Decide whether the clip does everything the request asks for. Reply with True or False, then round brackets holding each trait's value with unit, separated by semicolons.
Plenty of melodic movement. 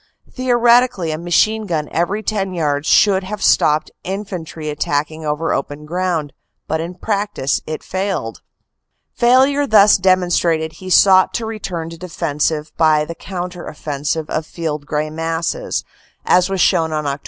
False (4.1 semitones)